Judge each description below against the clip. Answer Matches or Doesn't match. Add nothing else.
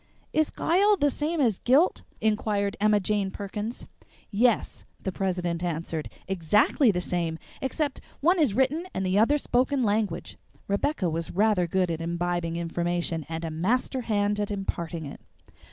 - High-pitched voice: Matches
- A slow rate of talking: Doesn't match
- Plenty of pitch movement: Matches